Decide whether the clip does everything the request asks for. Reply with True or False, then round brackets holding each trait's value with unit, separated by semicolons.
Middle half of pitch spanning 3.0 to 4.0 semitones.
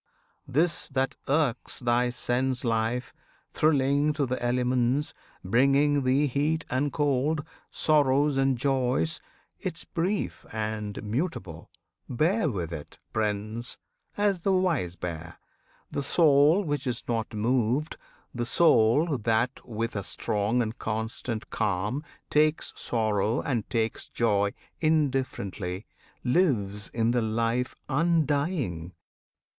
False (4.8 semitones)